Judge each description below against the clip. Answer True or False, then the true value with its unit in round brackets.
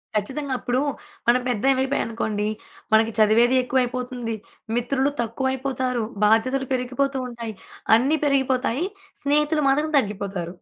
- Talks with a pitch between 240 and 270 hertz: True (250 Hz)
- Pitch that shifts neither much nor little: True (3.1 semitones)